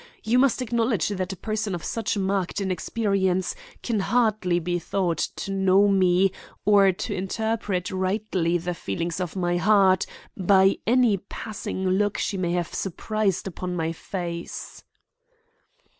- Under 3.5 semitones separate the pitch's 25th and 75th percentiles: Yes, average, 2.8 semitones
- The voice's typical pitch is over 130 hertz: Yes, high, 190 Hz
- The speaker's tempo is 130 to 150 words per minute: Yes, average, 140 wpm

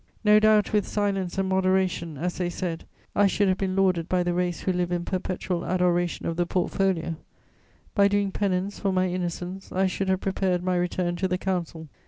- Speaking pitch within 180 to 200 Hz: Yes, medium, 185 Hz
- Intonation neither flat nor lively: No, narrow, 1.5 semitones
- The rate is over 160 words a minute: Yes, average, 200 wpm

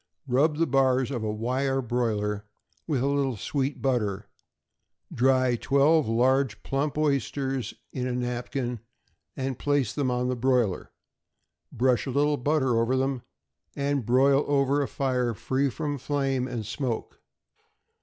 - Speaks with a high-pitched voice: No, low, 130 Hz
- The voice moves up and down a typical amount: No, narrow, 2.3 semitones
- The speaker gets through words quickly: No, average, 145 wpm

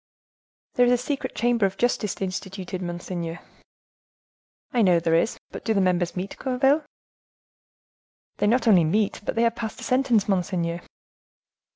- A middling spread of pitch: Yes, average, 5.0 semitones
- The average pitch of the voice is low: No, high, 200 Hz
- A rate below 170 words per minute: Yes, average, 155 wpm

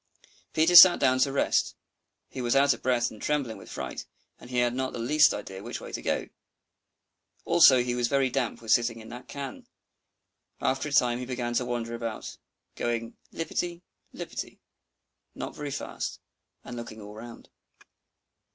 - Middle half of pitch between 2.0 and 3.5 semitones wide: Yes, average, 2.7 semitones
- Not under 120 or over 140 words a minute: No, average, 170 wpm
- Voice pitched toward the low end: Yes, low, 125 Hz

